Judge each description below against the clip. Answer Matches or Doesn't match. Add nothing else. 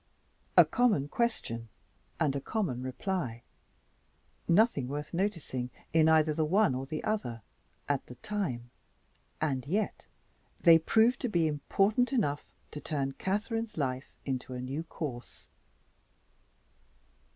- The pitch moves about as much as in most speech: Doesn't match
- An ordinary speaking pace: Doesn't match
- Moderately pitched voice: Matches